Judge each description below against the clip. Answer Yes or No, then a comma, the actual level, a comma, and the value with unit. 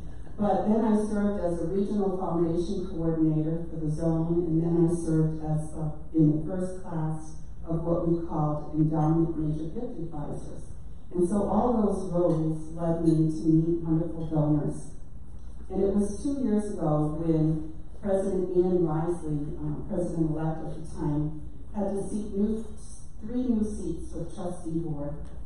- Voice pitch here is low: No, medium, 165 Hz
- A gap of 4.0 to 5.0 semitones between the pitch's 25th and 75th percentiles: No, average, 3.2 semitones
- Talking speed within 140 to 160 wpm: Yes, average, 155 wpm